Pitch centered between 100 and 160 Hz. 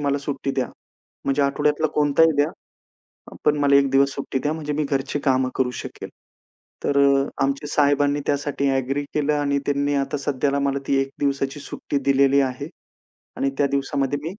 Yes: medium, 140 Hz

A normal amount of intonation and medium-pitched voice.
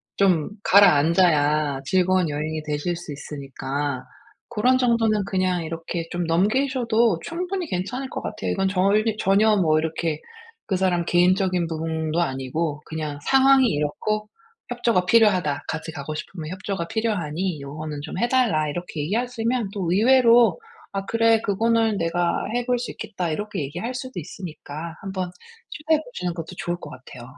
No: wide, 6.0 semitones; medium, 180 Hz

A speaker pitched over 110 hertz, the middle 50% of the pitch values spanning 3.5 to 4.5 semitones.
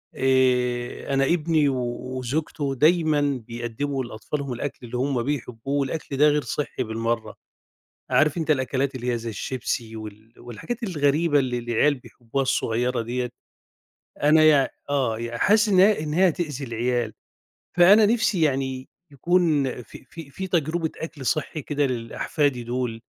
Yes: low, 135 Hz; average, 4.1 semitones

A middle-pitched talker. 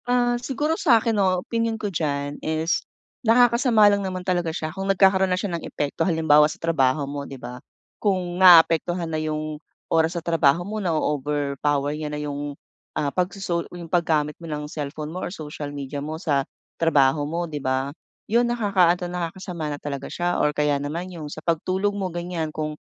Yes: medium, 165 Hz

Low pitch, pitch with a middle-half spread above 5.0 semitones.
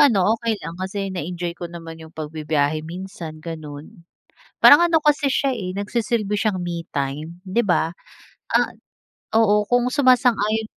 No: medium, 185 Hz; wide, 5.5 semitones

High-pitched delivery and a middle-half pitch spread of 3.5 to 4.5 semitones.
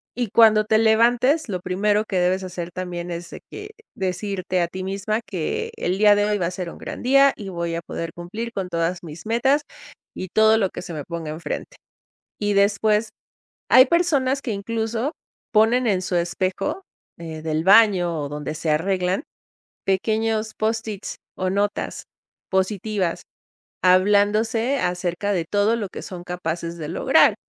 Yes: high, 195 Hz; average, 3.9 semitones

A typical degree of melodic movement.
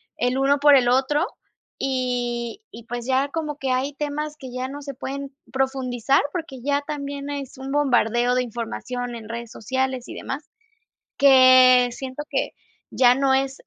No: narrow, 2.2 semitones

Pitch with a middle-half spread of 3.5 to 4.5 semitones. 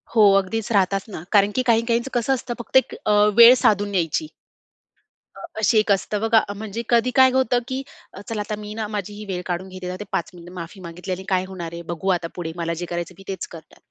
Yes: average, 3.9 semitones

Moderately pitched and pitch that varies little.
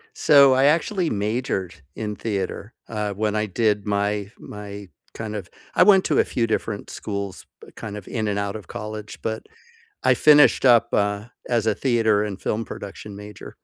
No: low, 105 Hz; narrow, 2.2 semitones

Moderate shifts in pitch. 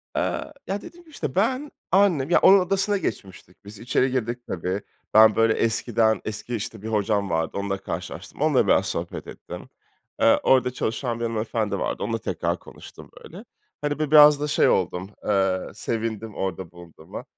No: wide, 6.6 semitones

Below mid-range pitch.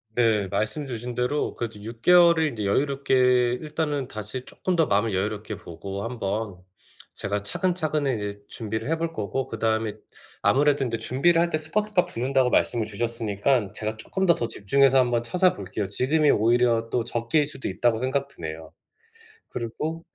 Yes: low, 120 Hz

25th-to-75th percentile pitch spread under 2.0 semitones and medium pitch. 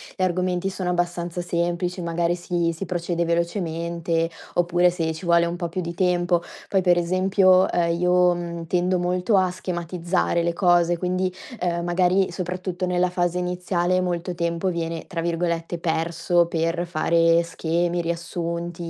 Yes: narrow, 1.0 semitones; medium, 175 Hz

